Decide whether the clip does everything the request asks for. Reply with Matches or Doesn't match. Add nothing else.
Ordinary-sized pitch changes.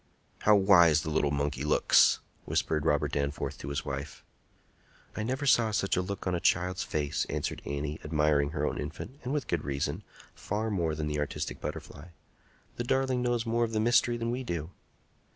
Doesn't match